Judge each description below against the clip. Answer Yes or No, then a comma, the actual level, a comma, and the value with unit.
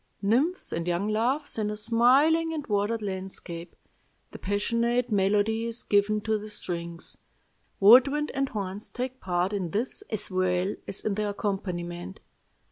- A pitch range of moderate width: Yes, average, 3.7 semitones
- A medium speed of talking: Yes, average, 150 wpm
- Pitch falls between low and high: No, high, 210 Hz